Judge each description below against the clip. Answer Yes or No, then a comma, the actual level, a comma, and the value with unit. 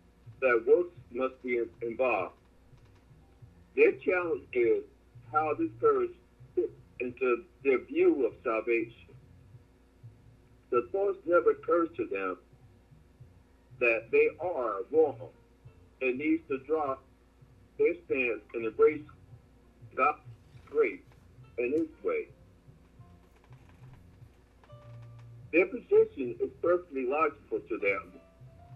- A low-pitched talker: Yes, low, 130 Hz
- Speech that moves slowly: Yes, slow, 100 wpm